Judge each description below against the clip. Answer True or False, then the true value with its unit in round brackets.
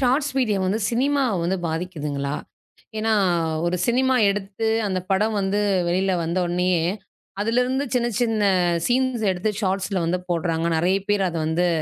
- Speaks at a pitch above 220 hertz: False (195 Hz)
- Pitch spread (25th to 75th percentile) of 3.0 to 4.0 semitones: False (4.7 semitones)